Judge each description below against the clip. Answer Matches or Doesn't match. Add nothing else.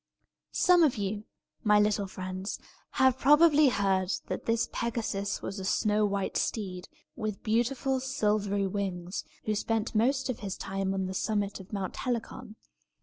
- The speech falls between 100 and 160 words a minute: Matches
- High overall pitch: Matches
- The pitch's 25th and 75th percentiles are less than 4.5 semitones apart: Matches